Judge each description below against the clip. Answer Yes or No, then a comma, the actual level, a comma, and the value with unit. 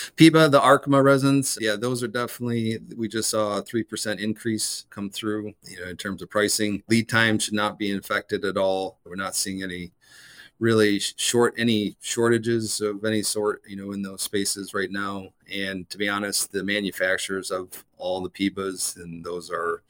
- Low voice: Yes, low, 105 Hz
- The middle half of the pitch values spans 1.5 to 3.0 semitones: Yes, average, 2.7 semitones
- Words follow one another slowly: No, average, 185 wpm